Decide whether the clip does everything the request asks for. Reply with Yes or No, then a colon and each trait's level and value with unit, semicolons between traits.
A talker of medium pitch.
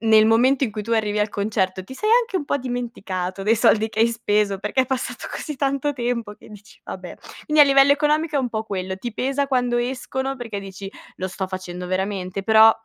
No: high, 225 Hz